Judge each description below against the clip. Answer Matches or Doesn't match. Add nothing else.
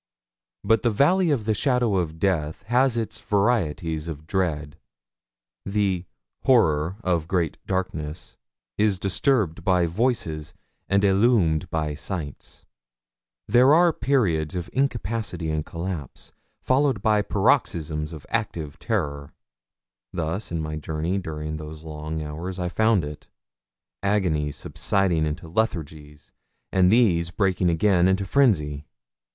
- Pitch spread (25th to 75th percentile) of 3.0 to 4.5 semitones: Doesn't match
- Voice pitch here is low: Matches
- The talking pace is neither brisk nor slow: Doesn't match